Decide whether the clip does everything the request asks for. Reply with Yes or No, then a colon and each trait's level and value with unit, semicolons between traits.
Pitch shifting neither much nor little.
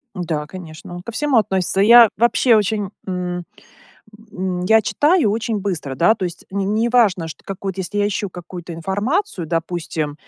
Yes: average, 3.8 semitones